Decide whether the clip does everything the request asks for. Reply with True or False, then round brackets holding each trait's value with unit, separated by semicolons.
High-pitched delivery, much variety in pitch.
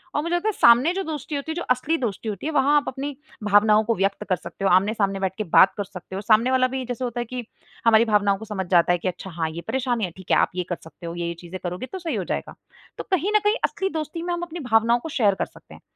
True (225 Hz; 6.7 semitones)